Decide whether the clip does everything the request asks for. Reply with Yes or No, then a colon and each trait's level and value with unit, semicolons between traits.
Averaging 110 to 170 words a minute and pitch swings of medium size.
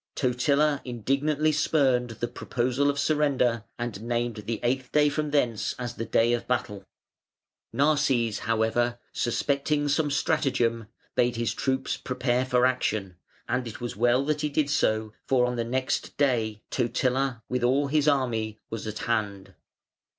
Yes: average, 150 wpm; average, 3.3 semitones